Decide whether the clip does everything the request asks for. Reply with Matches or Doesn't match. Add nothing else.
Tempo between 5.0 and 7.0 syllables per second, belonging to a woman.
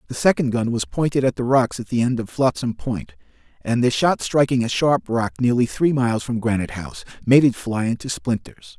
Doesn't match